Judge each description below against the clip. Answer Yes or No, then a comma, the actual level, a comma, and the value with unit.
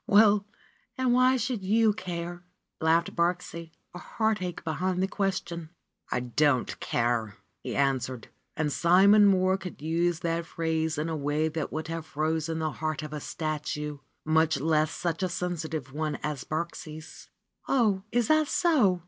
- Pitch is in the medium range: Yes, medium, 165 Hz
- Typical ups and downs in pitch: Yes, average, 3.4 semitones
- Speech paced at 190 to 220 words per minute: No, average, 155 wpm